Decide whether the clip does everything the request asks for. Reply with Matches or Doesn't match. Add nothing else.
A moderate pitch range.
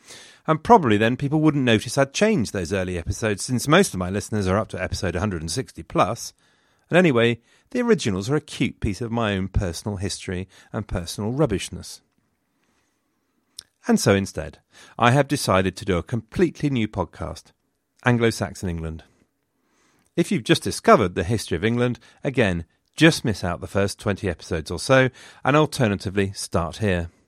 Doesn't match